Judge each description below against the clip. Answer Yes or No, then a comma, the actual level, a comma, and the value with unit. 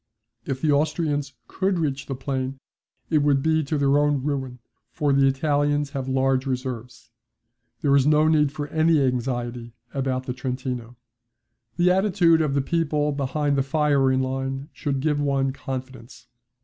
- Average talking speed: Yes, average, 155 wpm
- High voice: No, medium, 140 Hz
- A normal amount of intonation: No, narrow, 2.2 semitones